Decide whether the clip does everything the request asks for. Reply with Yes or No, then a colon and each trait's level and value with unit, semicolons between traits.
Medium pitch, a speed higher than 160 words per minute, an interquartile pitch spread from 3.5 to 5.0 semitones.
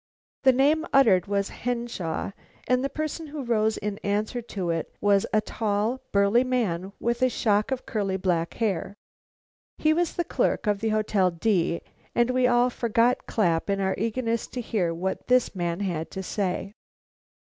No: high, 215 Hz; average, 170 wpm; average, 4.4 semitones